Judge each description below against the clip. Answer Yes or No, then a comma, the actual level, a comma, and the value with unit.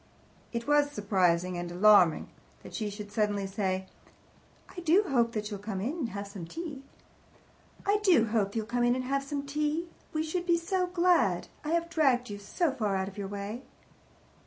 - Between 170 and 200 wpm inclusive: Yes, average, 195 wpm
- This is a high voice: Yes, high, 235 Hz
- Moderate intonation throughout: No, wide, 7.3 semitones